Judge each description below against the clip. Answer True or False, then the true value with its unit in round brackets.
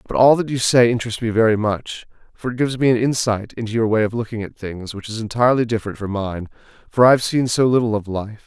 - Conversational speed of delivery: False (255 wpm)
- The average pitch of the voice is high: False (115 Hz)